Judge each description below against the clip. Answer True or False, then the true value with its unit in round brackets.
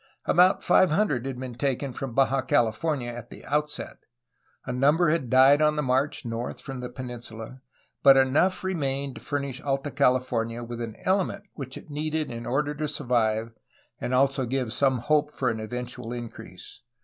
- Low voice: True (130 Hz)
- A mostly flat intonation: False (3.3 semitones)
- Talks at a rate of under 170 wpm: False (175 wpm)